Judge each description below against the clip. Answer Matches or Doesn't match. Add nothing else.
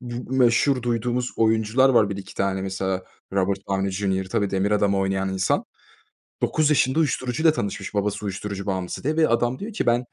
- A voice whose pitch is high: Doesn't match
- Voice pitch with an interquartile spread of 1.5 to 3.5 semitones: Doesn't match